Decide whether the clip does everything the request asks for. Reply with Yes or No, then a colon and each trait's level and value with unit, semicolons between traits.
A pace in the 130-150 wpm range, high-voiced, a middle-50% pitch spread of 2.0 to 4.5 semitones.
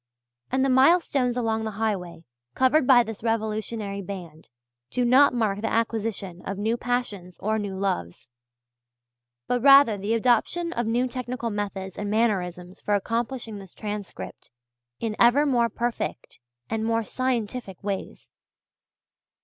Yes: slow, 135 wpm; high, 225 Hz; average, 3.4 semitones